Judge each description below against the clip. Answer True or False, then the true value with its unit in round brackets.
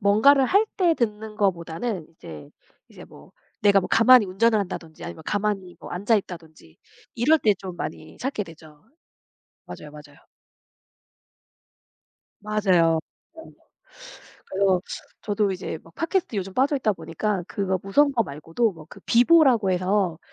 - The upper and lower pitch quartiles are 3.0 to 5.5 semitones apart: True (5.2 semitones)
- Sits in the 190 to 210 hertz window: True (200 Hz)